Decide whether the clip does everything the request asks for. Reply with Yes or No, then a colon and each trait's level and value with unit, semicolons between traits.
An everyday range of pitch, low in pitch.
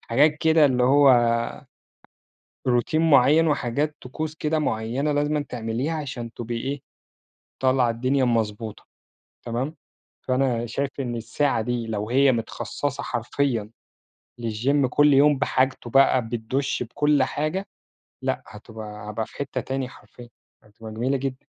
Yes: average, 3.7 semitones; low, 130 Hz